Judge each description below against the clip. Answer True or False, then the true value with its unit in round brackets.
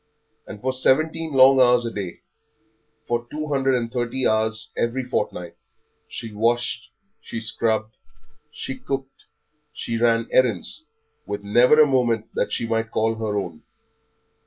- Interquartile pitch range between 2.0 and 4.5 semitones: True (2.9 semitones)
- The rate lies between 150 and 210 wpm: False (140 wpm)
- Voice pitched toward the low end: True (120 Hz)